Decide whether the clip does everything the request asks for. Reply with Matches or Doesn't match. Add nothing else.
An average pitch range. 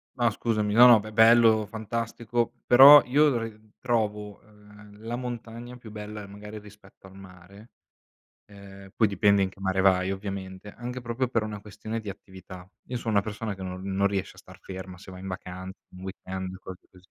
Matches